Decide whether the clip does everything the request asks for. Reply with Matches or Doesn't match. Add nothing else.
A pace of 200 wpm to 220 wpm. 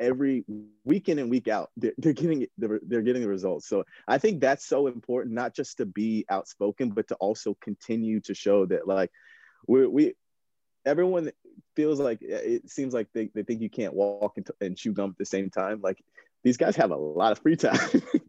Matches